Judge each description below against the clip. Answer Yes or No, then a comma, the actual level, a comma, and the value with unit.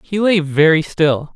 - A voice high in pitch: No, medium, 165 Hz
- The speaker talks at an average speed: Yes, average, 175 wpm